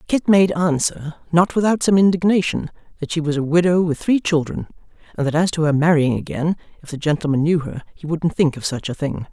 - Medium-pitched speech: Yes, medium, 165 Hz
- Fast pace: Yes, fast, 220 wpm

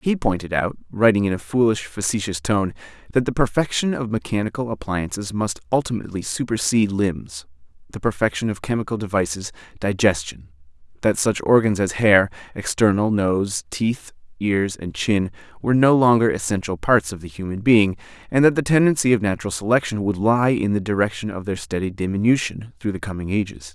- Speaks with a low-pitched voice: Yes, low, 105 Hz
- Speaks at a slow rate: No, average, 160 wpm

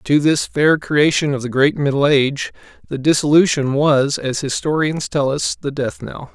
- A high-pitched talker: No, medium, 145 Hz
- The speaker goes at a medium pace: Yes, average, 180 wpm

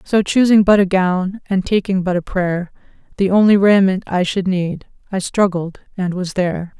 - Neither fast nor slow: Yes, average, 185 wpm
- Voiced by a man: No, female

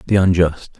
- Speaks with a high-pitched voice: No, very low, 90 Hz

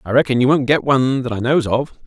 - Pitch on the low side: Yes, low, 130 Hz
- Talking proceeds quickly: Yes, fast, 290 wpm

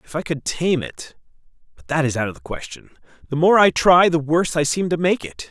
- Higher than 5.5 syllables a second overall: Yes, 5.7 syllables/s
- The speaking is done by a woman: No, male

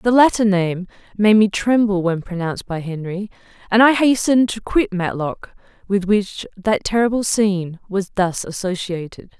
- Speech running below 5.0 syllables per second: Yes, 4.8 syllables/s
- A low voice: No, high, 200 Hz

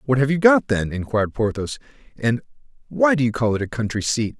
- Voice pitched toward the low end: Yes, low, 125 Hz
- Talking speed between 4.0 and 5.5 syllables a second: No, 6.0 syllables/s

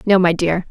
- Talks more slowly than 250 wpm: No, fast, 255 wpm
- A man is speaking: No, female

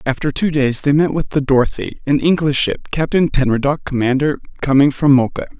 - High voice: No, medium, 140 Hz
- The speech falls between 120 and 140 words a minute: No, average, 180 wpm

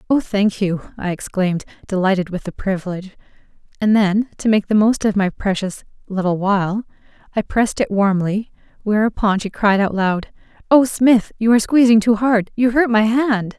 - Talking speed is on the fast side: No, average, 170 wpm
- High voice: Yes, high, 210 Hz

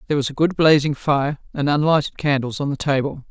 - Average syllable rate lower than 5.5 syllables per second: No, 6.0 syllables/s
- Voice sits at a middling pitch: Yes, medium, 145 Hz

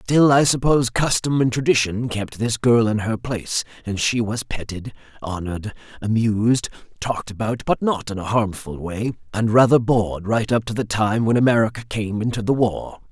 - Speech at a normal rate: Yes, average, 185 wpm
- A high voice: No, low, 115 Hz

